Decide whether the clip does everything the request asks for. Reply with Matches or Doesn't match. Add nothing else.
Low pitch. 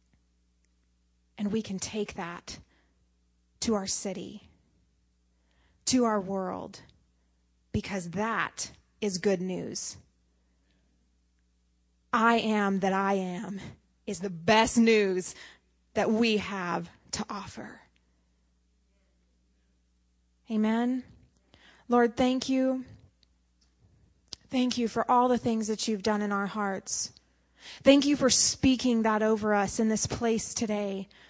Doesn't match